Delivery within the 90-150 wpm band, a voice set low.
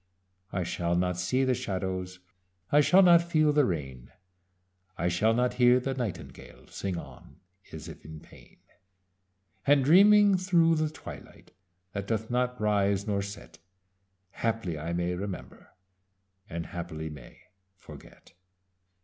Yes: slow, 135 wpm; low, 100 Hz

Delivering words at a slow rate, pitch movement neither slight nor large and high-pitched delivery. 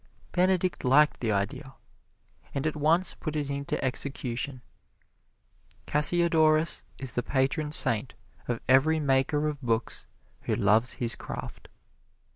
No: slow, 120 wpm; average, 3.7 semitones; medium, 140 Hz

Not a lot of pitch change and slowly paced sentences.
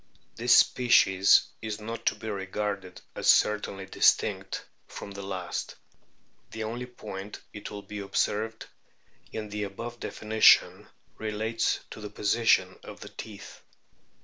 Yes: narrow, 2.1 semitones; slow, 130 wpm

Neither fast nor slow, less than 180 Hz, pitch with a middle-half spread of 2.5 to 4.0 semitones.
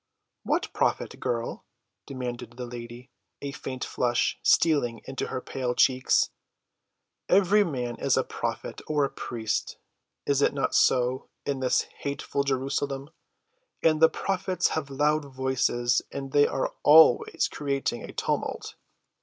No: slow, 130 wpm; low, 135 Hz; average, 2.8 semitones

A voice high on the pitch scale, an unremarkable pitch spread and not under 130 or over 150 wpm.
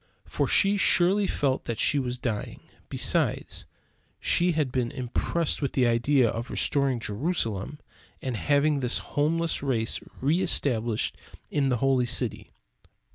No: low, 135 Hz; average, 3.9 semitones; slow, 135 wpm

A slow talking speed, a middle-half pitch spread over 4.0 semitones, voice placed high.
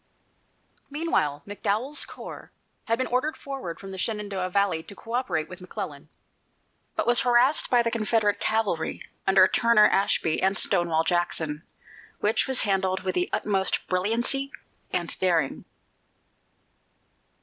Yes: slow, 125 wpm; average, 4.4 semitones; high, 200 Hz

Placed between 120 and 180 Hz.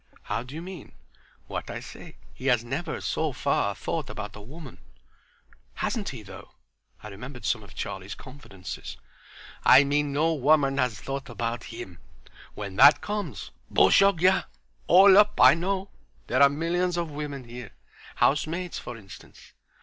Yes: medium, 140 Hz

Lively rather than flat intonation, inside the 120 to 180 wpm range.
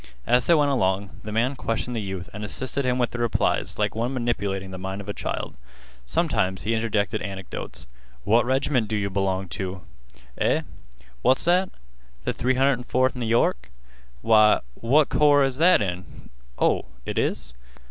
No: average, 4.8 semitones; average, 165 wpm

